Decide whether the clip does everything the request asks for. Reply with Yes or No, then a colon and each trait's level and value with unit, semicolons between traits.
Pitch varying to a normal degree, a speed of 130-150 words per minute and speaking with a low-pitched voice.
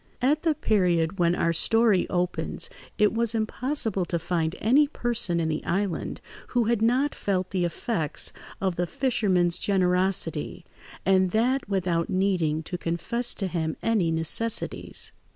No: average, 4.8 semitones; average, 145 wpm; high, 190 Hz